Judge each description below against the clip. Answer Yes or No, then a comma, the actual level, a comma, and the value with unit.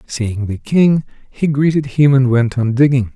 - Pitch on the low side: Yes, low, 130 Hz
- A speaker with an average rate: Yes, average, 190 wpm